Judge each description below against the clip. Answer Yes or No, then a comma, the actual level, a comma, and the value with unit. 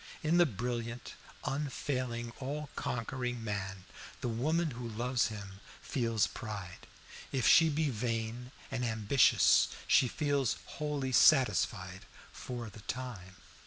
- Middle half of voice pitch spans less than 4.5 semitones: Yes, average, 3.3 semitones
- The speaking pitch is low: Yes, low, 120 Hz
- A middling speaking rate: No, slow, 120 wpm